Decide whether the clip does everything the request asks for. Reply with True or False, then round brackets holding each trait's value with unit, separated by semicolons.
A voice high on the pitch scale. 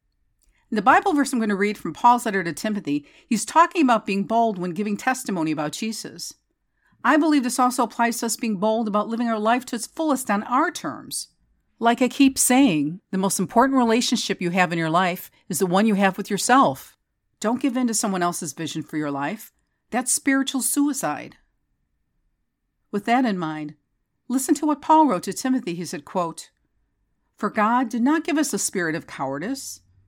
True (225 Hz)